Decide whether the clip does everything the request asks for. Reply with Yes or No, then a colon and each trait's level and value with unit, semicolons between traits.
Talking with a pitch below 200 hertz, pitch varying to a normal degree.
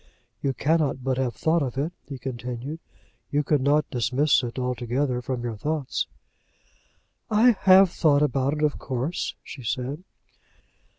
Yes: low, 135 Hz; average, 3.3 semitones